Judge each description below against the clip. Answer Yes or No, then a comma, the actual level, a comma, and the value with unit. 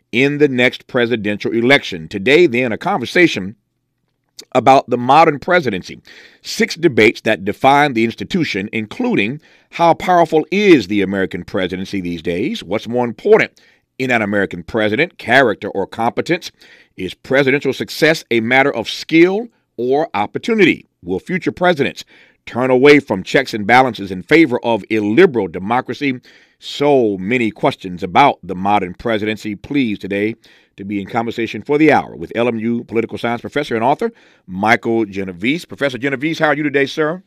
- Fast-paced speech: No, average, 150 wpm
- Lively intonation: Yes, wide, 5.7 semitones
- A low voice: Yes, low, 120 Hz